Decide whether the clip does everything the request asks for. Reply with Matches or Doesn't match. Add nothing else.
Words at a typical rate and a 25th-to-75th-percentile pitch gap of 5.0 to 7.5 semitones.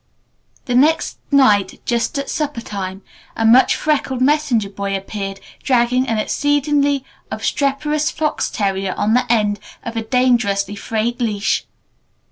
Doesn't match